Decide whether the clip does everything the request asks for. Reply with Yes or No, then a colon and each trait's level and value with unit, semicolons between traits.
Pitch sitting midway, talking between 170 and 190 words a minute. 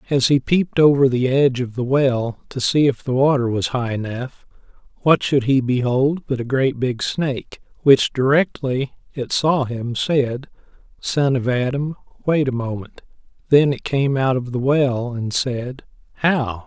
No: low, 130 Hz; average, 175 wpm